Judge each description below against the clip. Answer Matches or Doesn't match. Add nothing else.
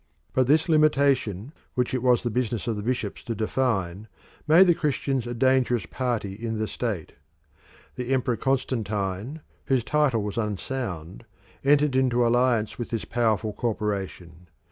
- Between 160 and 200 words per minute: Doesn't match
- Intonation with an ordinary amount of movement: Matches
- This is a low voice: Matches